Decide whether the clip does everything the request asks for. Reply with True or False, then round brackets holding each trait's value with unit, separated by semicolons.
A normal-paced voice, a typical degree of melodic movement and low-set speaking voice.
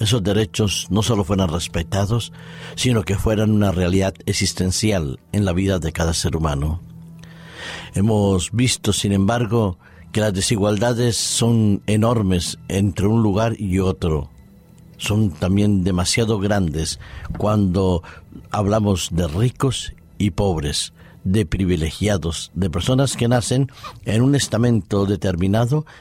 False (120 wpm; 3.7 semitones; 100 Hz)